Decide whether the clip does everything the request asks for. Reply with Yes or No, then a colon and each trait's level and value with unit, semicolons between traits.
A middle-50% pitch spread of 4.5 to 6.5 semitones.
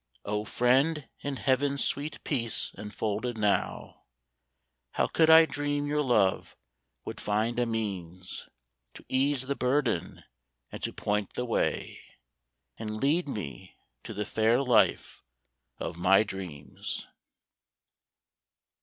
Yes: average, 5.2 semitones